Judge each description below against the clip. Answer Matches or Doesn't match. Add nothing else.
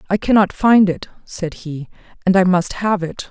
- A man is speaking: Doesn't match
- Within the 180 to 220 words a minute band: Matches